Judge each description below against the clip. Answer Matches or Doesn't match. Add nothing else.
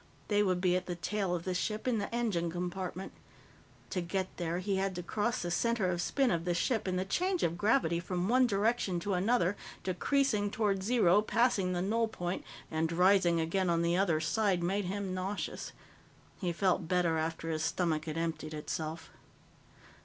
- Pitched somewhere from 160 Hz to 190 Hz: Matches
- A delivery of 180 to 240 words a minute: Matches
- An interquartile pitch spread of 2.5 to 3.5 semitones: Matches